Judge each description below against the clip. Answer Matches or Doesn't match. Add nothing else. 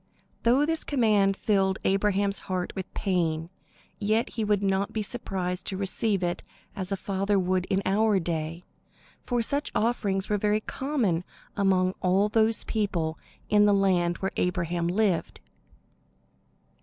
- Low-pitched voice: Doesn't match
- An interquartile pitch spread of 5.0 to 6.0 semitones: Doesn't match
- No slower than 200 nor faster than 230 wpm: Doesn't match